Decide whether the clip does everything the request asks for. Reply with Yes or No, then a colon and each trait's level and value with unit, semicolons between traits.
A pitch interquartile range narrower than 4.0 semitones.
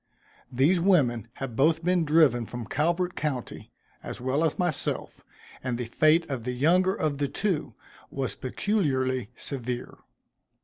No: average, 5.0 semitones